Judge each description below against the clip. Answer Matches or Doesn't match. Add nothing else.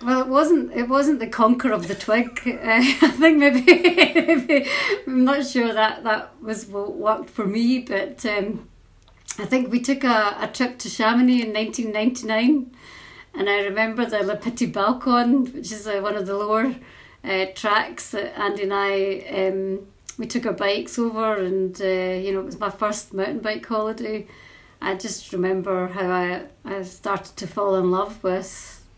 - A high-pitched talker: Matches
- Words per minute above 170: Matches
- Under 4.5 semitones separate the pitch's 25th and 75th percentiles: Matches